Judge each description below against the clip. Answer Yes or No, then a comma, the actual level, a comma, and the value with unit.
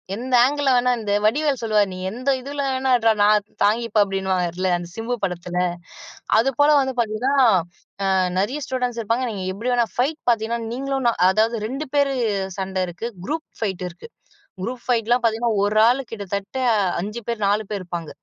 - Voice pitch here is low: No, high, 230 Hz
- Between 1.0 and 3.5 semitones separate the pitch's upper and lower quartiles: No, average, 4.1 semitones